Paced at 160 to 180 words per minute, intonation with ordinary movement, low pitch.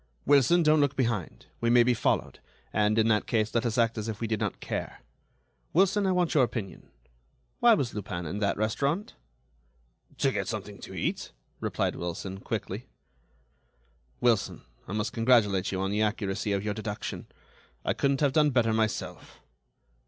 Yes: average, 170 wpm; average, 4.4 semitones; low, 115 Hz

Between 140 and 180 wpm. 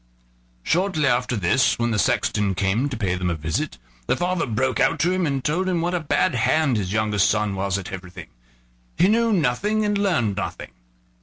No: average, 200 wpm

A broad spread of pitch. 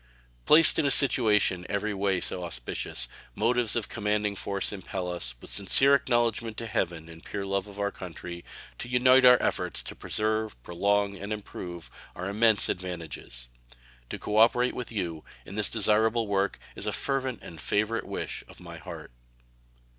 No: average, 3.9 semitones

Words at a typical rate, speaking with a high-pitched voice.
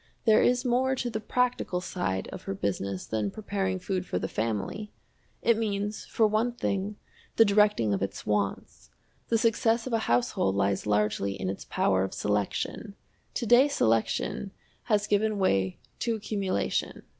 Yes: average, 160 wpm; high, 200 Hz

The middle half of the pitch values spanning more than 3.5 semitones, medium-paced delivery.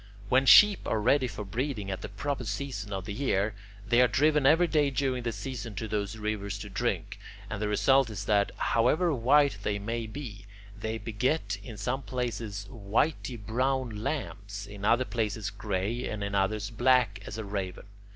Yes: average, 4.1 semitones; average, 180 wpm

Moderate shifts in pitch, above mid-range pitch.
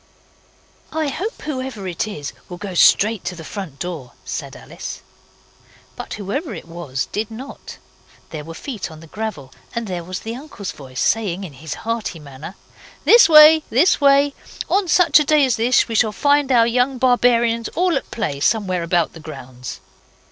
No: wide, 7.8 semitones; high, 220 Hz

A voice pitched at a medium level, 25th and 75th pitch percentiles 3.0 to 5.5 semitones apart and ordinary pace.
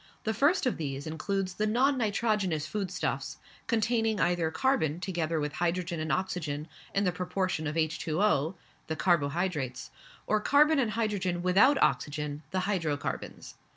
Yes: medium, 180 Hz; average, 5.2 semitones; average, 150 wpm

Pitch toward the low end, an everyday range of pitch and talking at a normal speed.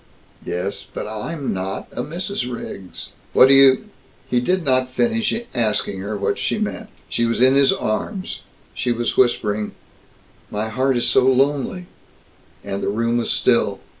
Yes: low, 125 Hz; average, 4.1 semitones; average, 165 wpm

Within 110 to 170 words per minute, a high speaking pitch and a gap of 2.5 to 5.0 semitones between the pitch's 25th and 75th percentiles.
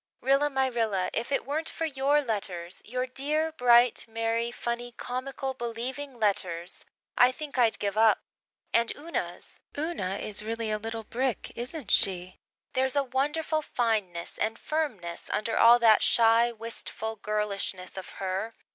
Yes: average, 145 wpm; high, 235 Hz; average, 3.9 semitones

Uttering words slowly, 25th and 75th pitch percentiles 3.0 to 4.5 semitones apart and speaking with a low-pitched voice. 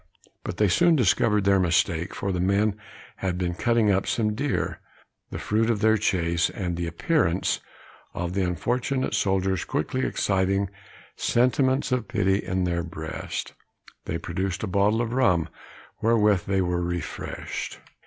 No: average, 150 wpm; average, 3.9 semitones; very low, 95 Hz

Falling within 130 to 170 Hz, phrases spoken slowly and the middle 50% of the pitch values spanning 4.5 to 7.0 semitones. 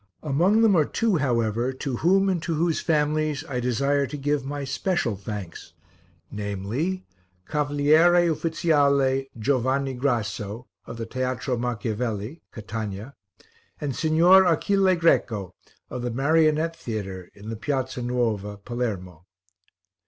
Yes: low, 135 Hz; slow, 125 wpm; wide, 5.6 semitones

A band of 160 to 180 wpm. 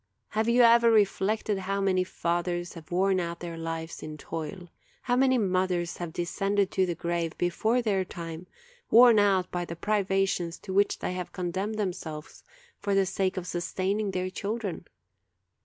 Yes: average, 165 wpm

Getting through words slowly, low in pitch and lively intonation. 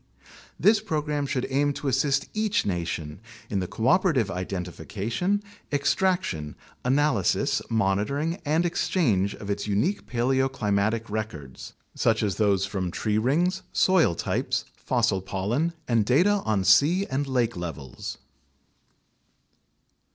Yes: slow, 115 wpm; low, 115 Hz; wide, 7.3 semitones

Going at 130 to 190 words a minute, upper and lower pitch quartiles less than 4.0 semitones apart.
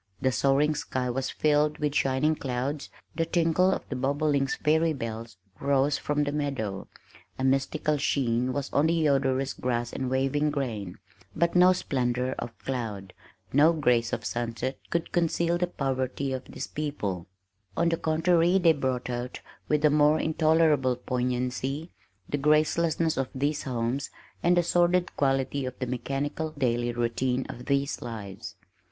Yes: average, 155 wpm; average, 3.5 semitones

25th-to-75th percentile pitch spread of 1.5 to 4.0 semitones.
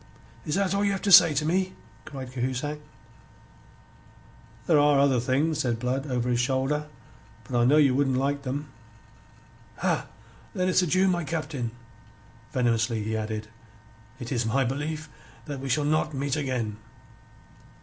Yes: average, 3.5 semitones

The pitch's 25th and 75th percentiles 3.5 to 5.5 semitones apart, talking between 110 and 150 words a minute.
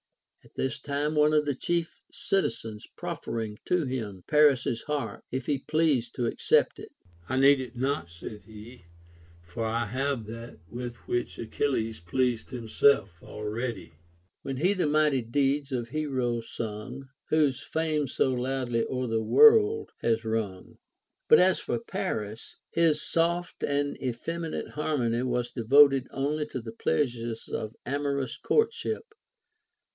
Yes: average, 4.3 semitones; average, 145 wpm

